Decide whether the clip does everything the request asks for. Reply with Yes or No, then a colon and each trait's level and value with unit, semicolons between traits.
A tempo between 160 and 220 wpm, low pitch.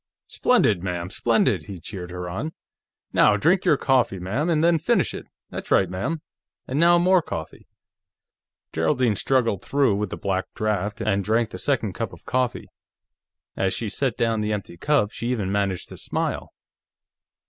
Yes: average, 170 wpm; low, 110 Hz